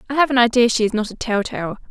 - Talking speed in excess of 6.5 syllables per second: Yes, 7.4 syllables/s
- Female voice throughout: Yes, female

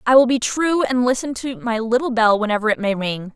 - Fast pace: Yes, fast, 250 wpm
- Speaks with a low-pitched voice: No, high, 235 Hz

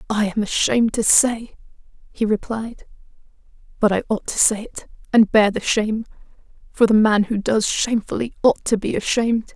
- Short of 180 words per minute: Yes, average, 170 wpm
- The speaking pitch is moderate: No, high, 220 Hz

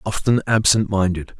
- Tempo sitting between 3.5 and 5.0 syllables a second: Yes, 4.9 syllables/s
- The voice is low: Yes, low, 100 Hz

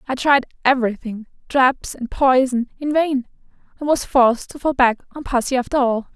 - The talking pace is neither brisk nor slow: Yes, average, 175 wpm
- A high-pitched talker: Yes, very high, 260 Hz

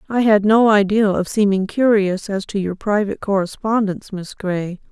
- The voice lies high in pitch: Yes, high, 200 Hz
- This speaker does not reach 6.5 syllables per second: Yes, 5.0 syllables/s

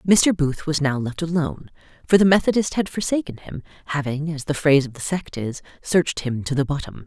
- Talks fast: Yes, fast, 210 wpm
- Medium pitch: Yes, medium, 150 Hz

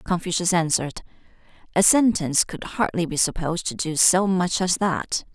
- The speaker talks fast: No, average, 155 wpm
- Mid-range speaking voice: Yes, medium, 175 Hz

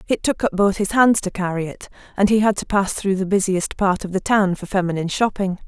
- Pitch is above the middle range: Yes, high, 195 Hz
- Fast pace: Yes, fast, 255 wpm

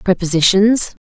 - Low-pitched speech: No, high, 190 Hz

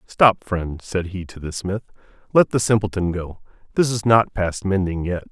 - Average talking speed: Yes, average, 190 wpm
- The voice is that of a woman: No, male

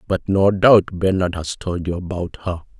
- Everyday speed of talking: Yes, average, 195 wpm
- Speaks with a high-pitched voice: No, very low, 90 Hz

